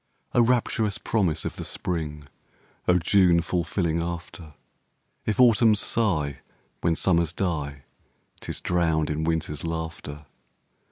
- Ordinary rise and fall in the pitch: Yes, average, 3.4 semitones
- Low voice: Yes, very low, 85 Hz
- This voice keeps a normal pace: No, slow, 115 wpm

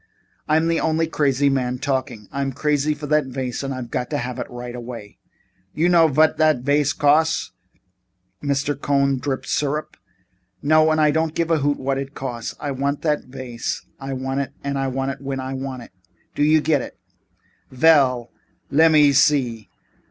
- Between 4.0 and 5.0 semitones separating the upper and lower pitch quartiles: No, narrow, 2.6 semitones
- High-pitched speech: No, medium, 140 Hz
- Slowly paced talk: No, average, 175 wpm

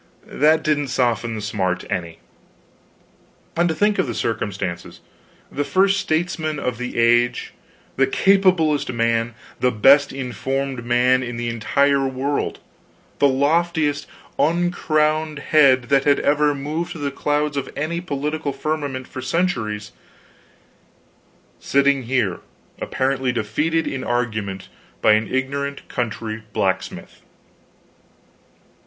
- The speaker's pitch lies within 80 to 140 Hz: Yes, low, 135 Hz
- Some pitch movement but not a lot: Yes, average, 4.4 semitones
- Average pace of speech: No, slow, 115 wpm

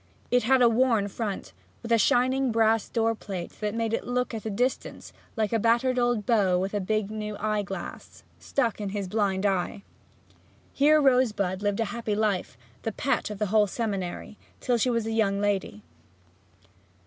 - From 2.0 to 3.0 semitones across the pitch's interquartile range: Yes, average, 2.7 semitones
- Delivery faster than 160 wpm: Yes, average, 185 wpm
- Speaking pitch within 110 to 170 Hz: No, high, 220 Hz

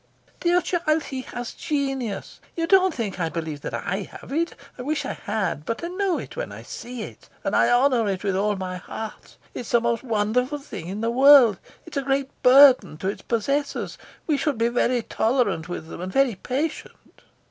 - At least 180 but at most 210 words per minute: Yes, average, 200 wpm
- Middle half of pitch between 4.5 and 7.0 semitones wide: Yes, wide, 5.6 semitones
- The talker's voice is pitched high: Yes, high, 245 Hz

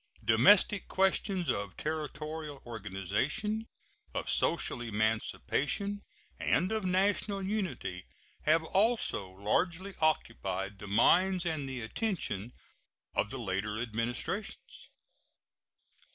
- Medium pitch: Yes, medium, 150 Hz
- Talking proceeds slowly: Yes, slow, 95 wpm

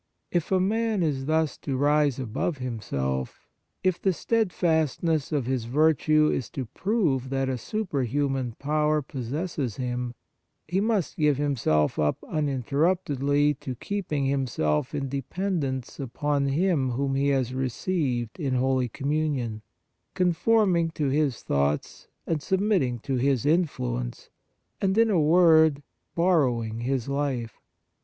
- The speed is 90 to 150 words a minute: Yes, slow, 135 wpm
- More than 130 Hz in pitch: Yes, medium, 140 Hz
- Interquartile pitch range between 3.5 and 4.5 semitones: Yes, average, 4.2 semitones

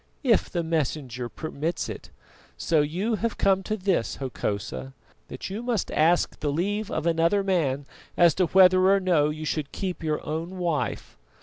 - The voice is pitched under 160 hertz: No, medium, 170 Hz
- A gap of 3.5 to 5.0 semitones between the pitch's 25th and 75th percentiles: Yes, average, 4.0 semitones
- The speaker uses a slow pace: No, average, 170 wpm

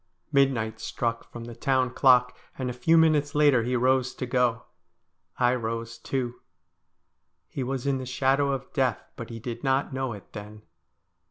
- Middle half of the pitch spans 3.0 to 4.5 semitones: No, narrow, 2.4 semitones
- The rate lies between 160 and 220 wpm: Yes, average, 170 wpm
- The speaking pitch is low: Yes, low, 125 Hz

